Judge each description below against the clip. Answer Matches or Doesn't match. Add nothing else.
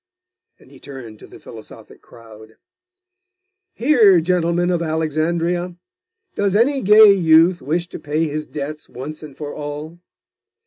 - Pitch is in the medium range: Matches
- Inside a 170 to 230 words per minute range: Doesn't match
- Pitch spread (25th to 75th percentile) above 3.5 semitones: Doesn't match